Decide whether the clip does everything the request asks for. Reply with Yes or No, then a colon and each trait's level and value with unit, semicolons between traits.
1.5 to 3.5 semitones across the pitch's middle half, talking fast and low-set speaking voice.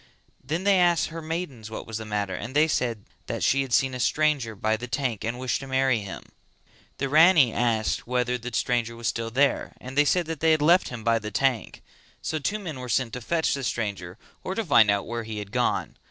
No: average, 5.0 semitones; fast, 235 wpm; low, 125 Hz